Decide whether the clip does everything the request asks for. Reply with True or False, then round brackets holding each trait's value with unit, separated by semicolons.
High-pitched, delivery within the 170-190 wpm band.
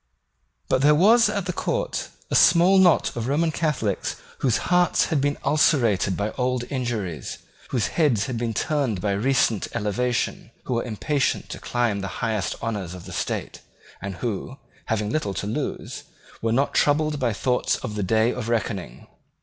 False (120 Hz; 175 wpm)